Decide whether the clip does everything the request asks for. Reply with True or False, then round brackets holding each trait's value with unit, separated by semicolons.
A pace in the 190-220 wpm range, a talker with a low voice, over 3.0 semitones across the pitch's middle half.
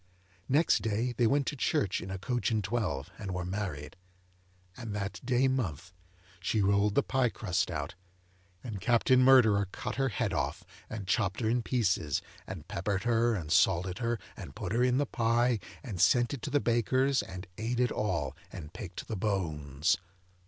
False (180 wpm; 110 Hz; 4.8 semitones)